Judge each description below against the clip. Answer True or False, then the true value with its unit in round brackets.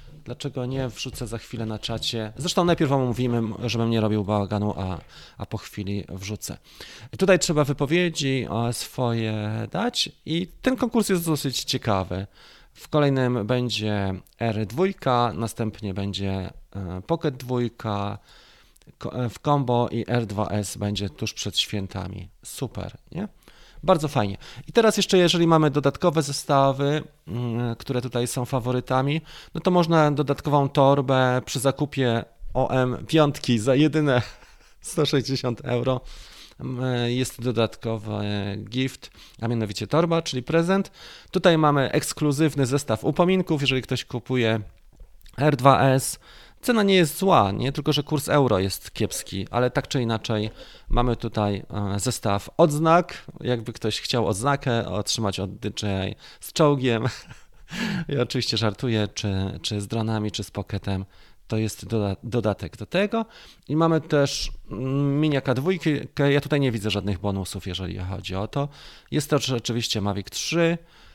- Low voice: True (125 Hz)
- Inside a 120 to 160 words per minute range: True (130 wpm)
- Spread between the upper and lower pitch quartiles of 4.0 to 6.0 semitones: True (5.5 semitones)